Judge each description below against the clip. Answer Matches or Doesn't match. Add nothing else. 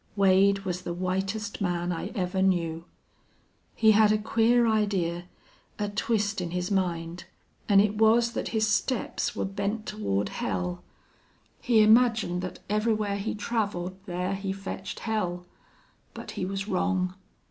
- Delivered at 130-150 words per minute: Matches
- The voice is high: Matches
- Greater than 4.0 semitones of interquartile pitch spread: Doesn't match